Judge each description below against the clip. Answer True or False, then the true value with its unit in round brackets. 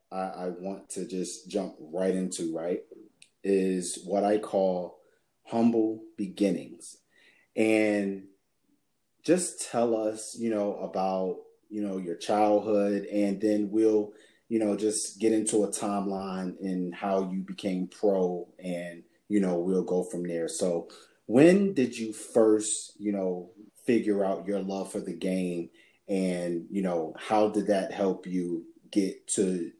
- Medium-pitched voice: False (100 Hz)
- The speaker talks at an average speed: True (145 wpm)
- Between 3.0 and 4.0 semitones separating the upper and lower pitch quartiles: False (2.5 semitones)